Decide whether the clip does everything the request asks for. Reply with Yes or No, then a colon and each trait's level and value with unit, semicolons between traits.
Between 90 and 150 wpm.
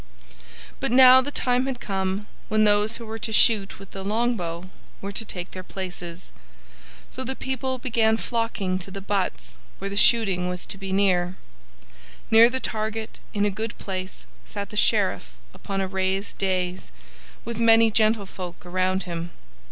No: average, 160 wpm